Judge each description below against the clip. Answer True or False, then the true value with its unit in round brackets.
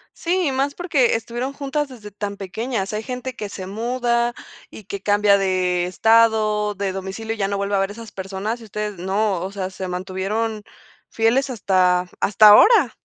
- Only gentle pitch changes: False (3.6 semitones)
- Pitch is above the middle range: True (210 Hz)